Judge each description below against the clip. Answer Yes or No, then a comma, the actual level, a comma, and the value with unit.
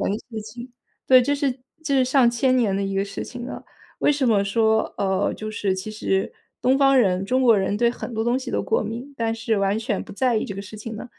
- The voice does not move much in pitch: No, average, 4.1 semitones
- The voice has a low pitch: No, high, 225 Hz